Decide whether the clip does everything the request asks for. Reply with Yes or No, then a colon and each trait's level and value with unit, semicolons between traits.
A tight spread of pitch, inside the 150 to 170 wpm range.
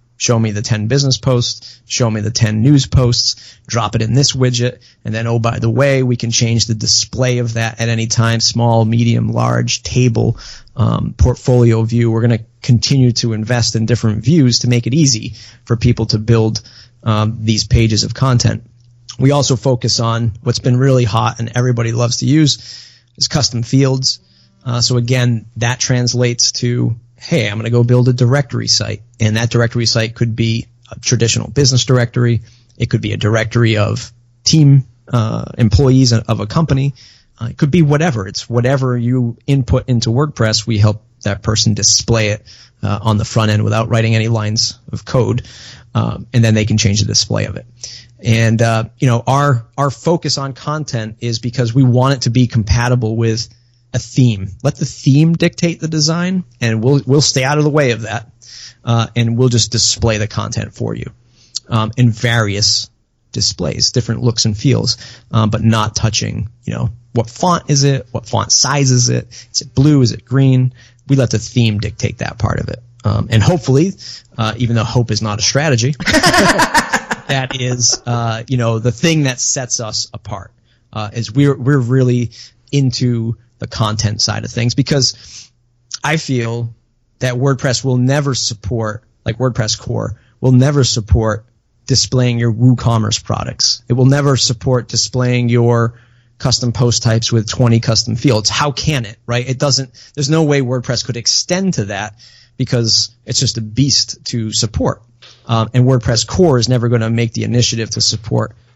No: narrow, 2.2 semitones; average, 185 wpm